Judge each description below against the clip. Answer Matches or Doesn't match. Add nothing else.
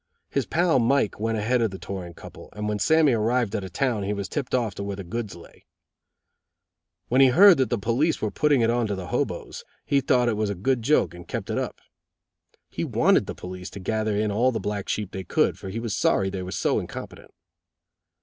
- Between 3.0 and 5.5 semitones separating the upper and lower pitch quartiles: Matches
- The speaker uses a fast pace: Matches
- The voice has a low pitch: Matches